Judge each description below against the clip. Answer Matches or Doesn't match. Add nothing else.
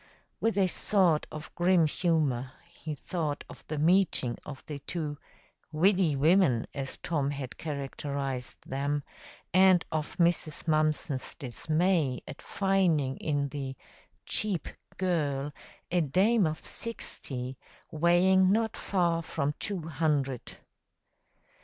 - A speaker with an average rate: Doesn't match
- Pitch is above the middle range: Doesn't match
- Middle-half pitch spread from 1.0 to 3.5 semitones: Doesn't match